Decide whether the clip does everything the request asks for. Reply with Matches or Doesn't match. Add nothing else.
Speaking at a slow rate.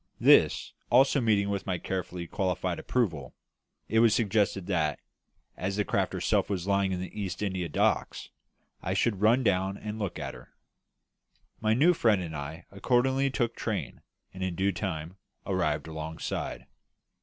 Doesn't match